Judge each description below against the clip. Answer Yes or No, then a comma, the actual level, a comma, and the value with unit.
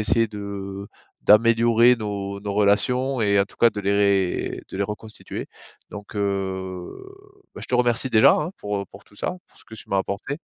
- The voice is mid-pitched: No, low, 105 Hz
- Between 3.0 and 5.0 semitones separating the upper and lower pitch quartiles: No, narrow, 2.5 semitones